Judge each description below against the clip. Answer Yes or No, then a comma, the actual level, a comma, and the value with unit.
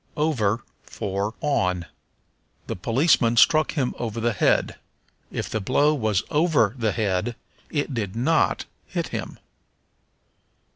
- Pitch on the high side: No, low, 115 Hz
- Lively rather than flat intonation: Yes, wide, 5.9 semitones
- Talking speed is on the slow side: Yes, slow, 125 wpm